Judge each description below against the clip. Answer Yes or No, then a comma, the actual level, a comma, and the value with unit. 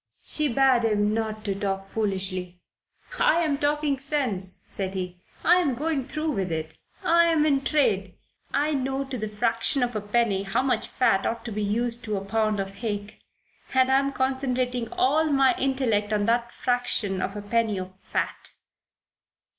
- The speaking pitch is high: Yes, high, 230 Hz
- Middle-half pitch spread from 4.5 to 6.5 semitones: Yes, average, 5.0 semitones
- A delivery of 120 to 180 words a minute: Yes, average, 160 wpm